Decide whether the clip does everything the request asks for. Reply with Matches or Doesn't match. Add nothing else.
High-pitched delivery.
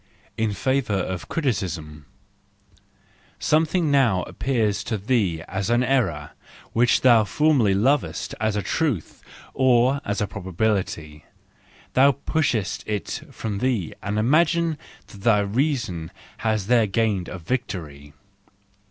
Doesn't match